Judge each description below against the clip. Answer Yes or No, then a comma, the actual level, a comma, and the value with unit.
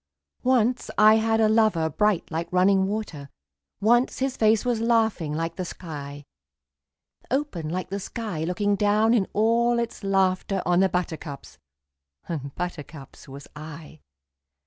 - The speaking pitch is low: No, high, 195 Hz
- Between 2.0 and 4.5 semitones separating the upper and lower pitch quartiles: No, average, 5.3 semitones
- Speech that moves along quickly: No, average, 140 wpm